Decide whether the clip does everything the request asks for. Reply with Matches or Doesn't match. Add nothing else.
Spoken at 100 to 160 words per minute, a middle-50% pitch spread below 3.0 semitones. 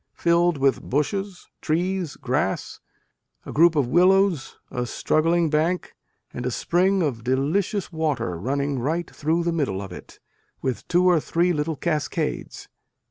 Doesn't match